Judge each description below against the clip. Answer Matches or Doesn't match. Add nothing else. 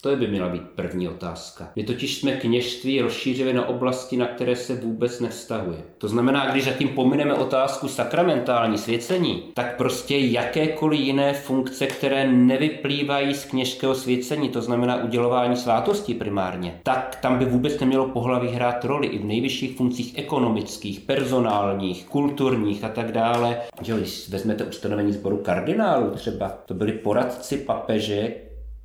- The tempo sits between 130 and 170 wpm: Matches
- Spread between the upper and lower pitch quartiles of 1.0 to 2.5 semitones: Doesn't match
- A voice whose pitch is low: Matches